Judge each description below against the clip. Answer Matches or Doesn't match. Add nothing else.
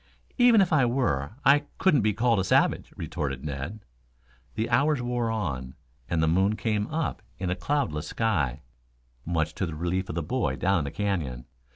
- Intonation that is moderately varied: Doesn't match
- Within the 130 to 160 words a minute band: Doesn't match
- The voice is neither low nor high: Doesn't match